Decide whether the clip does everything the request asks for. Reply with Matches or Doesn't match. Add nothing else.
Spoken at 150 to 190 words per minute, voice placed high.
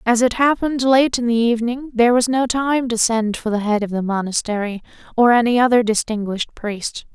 Doesn't match